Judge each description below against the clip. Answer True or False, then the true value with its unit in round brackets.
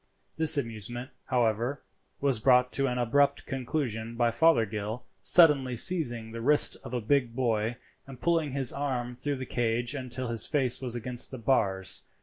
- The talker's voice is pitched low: True (125 Hz)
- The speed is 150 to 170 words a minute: True (160 wpm)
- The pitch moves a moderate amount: True (3.1 semitones)